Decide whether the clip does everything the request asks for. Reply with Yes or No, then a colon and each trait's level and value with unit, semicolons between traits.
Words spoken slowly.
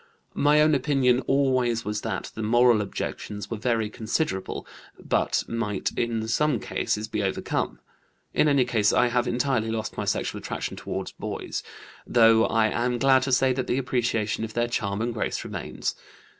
No: average, 170 wpm